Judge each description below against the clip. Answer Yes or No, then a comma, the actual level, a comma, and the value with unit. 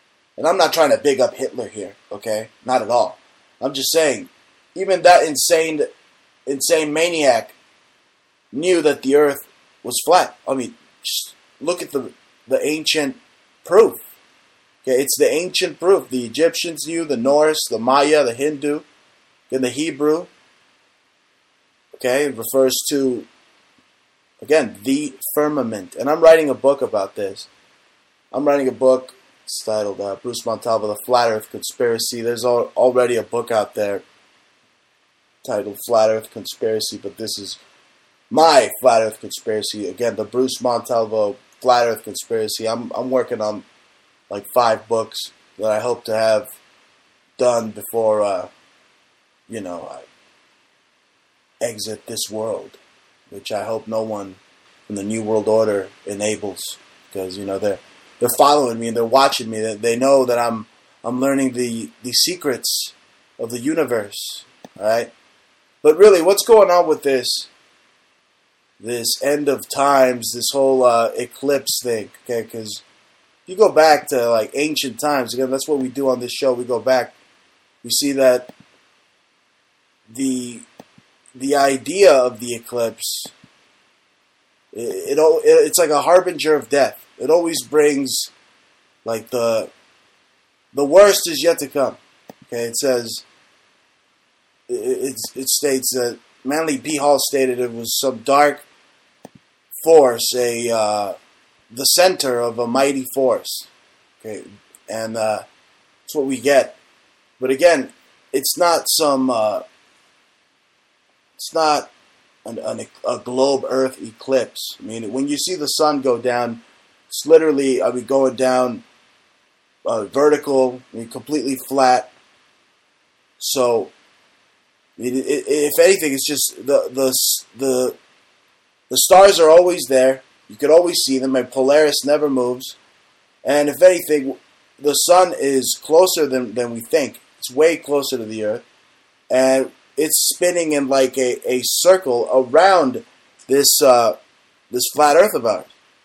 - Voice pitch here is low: Yes, low, 130 Hz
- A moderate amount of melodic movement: Yes, average, 4.1 semitones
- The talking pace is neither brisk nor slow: Yes, average, 145 wpm